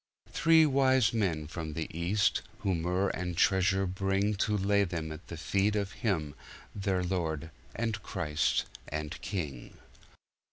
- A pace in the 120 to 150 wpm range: Yes, slow, 135 wpm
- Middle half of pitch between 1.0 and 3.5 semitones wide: No, average, 4.0 semitones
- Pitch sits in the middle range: No, very low, 95 Hz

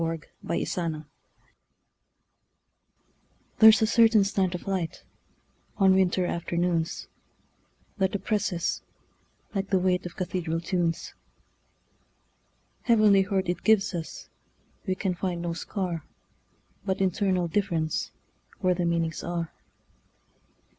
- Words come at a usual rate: No, slow, 90 wpm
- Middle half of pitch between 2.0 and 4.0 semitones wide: Yes, narrow, 2.4 semitones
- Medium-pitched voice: Yes, medium, 180 Hz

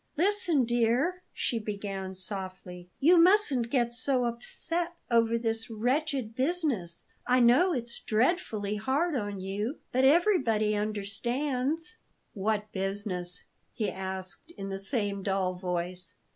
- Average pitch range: No, wide, 5.7 semitones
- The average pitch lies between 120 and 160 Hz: No, high, 230 Hz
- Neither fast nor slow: No, slow, 120 wpm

